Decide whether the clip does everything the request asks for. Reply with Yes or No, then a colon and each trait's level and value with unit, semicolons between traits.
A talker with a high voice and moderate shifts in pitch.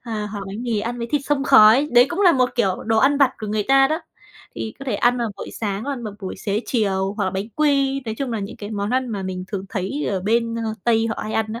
Yes: high, 230 Hz; average, 4.1 semitones